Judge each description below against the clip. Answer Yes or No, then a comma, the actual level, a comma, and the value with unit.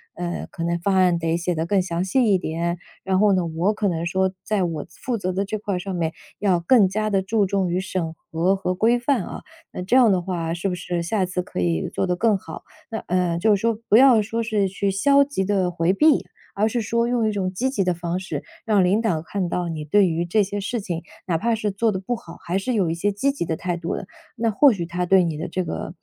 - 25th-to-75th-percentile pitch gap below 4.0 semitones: Yes, average, 3.6 semitones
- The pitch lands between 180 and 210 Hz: Yes, high, 190 Hz